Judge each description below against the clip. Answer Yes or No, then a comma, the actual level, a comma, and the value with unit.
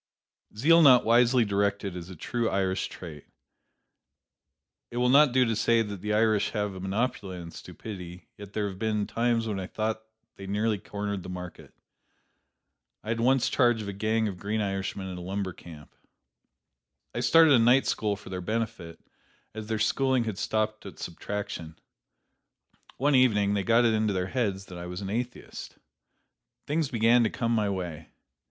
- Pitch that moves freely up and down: No, average, 3.3 semitones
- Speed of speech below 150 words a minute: No, average, 175 wpm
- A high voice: No, low, 105 Hz